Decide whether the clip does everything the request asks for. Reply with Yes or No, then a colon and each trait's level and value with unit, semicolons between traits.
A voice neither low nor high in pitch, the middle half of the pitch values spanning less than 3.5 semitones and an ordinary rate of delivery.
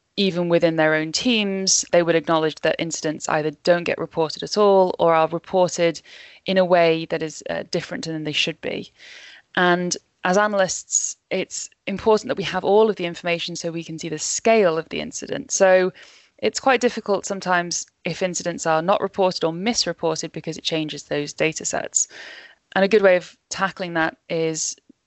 Yes: medium, 175 Hz; average, 3.0 semitones; average, 185 wpm